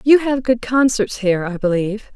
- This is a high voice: Yes, high, 225 Hz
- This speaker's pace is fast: No, average, 195 wpm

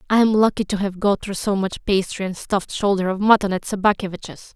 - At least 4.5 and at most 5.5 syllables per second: No, 6.0 syllables/s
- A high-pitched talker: Yes, high, 200 Hz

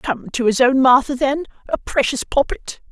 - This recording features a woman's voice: Yes, female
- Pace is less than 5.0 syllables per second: Yes, 4.7 syllables/s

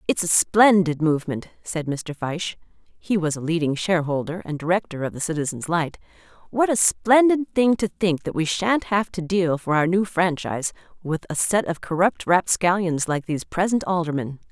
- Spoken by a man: No, female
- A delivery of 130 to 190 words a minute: Yes, average, 180 wpm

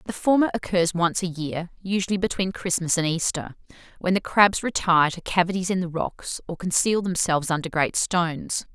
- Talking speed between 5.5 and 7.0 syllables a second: No, 5.3 syllables/s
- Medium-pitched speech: Yes, medium, 175 Hz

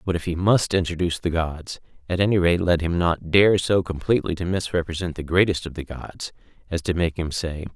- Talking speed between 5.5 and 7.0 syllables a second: Yes, 5.6 syllables/s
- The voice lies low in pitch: Yes, very low, 85 Hz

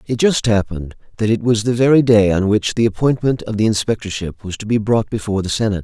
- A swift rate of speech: Yes, fast, 235 wpm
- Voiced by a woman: No, male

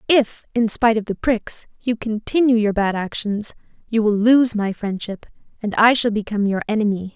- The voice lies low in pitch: No, high, 220 Hz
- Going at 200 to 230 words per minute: No, average, 185 wpm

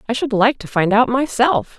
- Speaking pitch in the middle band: No, high, 240 Hz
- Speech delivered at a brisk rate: Yes, fast, 235 wpm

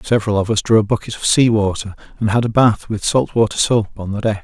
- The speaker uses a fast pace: Yes, fast, 270 wpm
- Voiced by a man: Yes, male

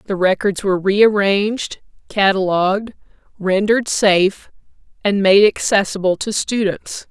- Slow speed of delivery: Yes, slow, 100 wpm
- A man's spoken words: No, female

